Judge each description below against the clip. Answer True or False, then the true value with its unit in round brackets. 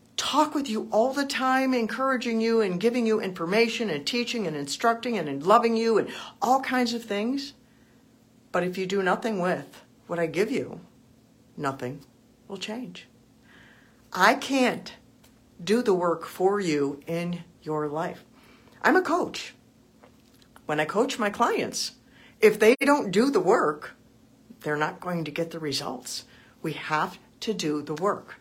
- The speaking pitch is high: True (205 Hz)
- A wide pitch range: True (6.6 semitones)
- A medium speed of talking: True (155 wpm)